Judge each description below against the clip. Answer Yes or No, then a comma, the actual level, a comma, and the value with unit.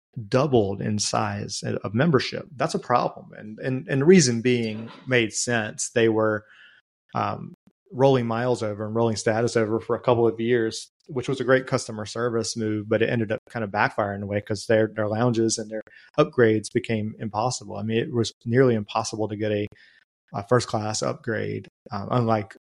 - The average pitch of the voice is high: No, low, 115 Hz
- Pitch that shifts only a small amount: Yes, narrow, 2.3 semitones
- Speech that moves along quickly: No, average, 190 wpm